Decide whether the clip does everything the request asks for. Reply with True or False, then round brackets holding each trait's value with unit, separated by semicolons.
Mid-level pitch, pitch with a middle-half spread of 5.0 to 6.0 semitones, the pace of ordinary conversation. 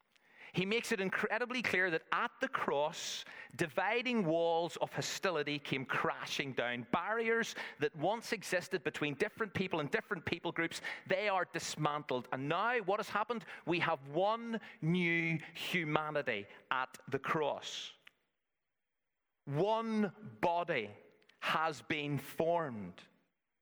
False (170 Hz; 5.5 semitones; 120 wpm)